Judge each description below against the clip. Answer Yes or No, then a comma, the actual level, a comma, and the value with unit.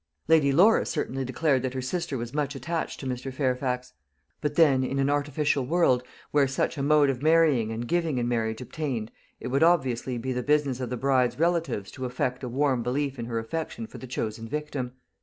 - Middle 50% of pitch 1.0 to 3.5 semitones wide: Yes, average, 3.0 semitones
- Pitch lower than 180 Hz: Yes, low, 135 Hz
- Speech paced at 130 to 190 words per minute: No, fast, 205 wpm